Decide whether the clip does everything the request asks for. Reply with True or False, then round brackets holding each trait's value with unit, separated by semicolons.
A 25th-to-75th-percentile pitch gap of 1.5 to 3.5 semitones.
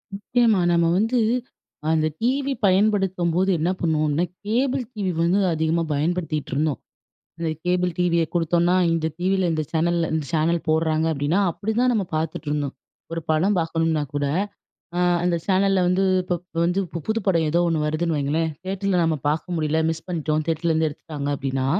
True (3.0 semitones)